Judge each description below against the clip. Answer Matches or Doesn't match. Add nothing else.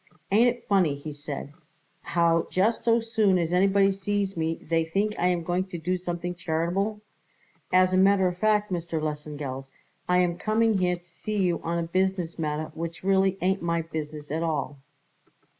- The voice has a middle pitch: Matches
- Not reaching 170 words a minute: Doesn't match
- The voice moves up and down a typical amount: Matches